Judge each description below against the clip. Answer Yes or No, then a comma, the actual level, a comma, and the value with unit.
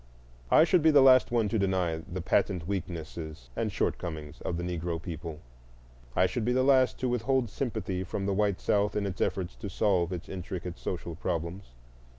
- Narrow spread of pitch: No, average, 4.2 semitones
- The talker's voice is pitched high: No, very low, 95 Hz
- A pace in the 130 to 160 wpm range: No, average, 185 wpm